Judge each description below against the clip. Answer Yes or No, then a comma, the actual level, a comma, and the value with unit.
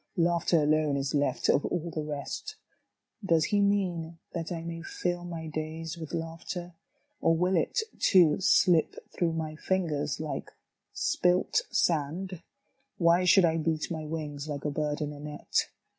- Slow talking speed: No, average, 160 wpm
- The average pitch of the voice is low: No, medium, 165 Hz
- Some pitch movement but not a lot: No, narrow, 2.3 semitones